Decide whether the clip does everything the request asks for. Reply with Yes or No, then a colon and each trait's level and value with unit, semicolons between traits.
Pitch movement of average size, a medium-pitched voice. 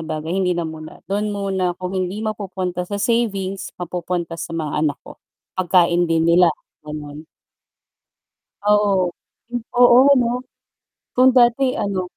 Yes: average, 3.2 semitones; medium, 180 Hz